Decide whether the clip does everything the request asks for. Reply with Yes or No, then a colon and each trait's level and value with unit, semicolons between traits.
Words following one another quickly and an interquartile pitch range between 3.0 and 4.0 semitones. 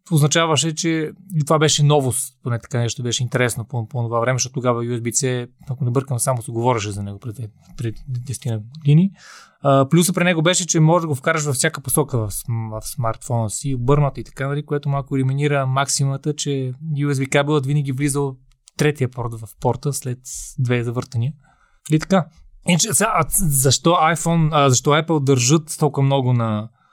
Yes: fast, 170 wpm; average, 3.7 semitones